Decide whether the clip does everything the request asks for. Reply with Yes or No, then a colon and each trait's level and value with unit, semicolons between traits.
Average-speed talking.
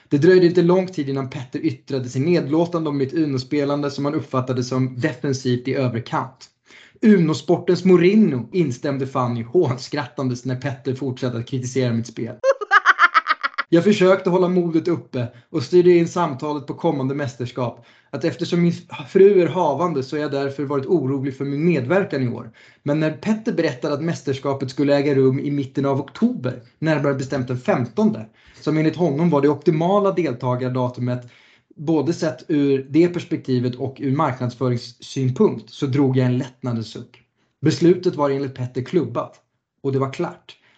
Yes: average, 155 wpm